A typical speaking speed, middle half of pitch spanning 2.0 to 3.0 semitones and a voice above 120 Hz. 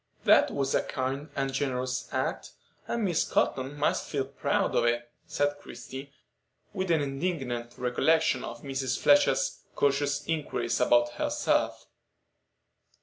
No: slow, 130 wpm; narrow, 2.5 semitones; low, 135 Hz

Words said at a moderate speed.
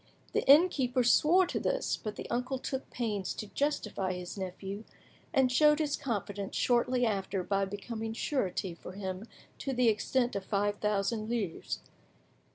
Yes: average, 155 wpm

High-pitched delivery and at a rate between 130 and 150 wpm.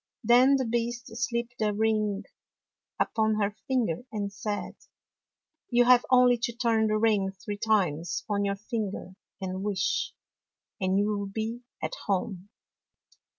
Yes: high, 215 Hz; average, 140 wpm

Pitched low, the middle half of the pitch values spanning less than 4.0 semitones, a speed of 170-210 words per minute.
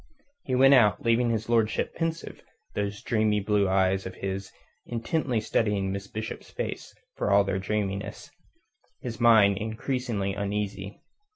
No: low, 105 Hz; average, 2.8 semitones; slow, 135 wpm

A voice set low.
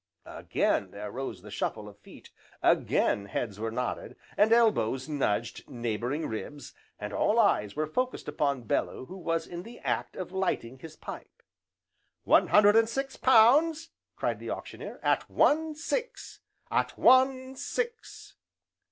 No: medium, 165 Hz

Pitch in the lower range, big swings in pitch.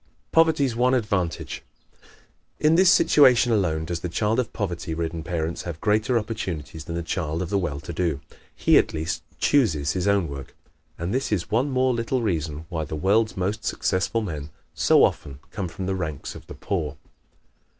Yes: very low, 95 Hz; wide, 5.8 semitones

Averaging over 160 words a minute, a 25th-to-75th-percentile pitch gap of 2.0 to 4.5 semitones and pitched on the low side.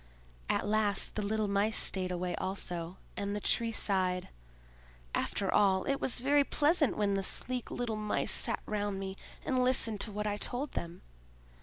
No: average, 170 wpm; average, 3.3 semitones; high, 205 Hz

